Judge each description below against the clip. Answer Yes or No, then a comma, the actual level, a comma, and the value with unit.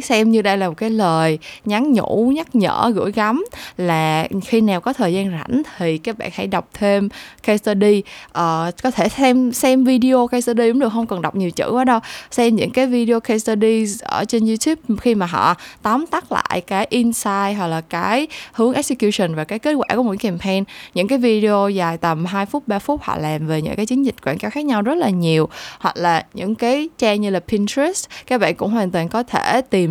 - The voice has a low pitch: No, high, 220 Hz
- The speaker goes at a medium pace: Yes, average, 225 wpm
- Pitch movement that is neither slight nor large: Yes, average, 4.6 semitones